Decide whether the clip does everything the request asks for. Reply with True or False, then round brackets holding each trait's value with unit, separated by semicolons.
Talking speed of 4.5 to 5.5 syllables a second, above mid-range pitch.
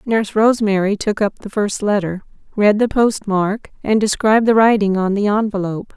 True (5.4 syllables/s; 210 Hz)